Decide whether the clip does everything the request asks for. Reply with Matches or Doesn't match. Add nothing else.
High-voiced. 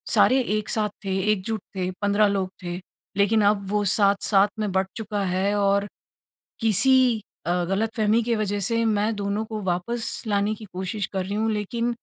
Matches